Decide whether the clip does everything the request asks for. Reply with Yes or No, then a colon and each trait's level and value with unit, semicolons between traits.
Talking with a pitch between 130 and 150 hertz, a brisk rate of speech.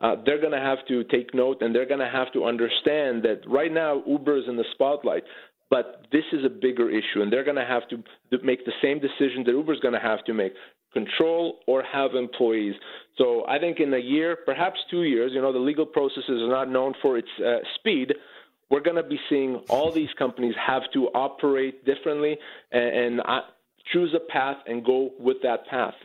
Yes: low, 135 Hz; fast, 215 wpm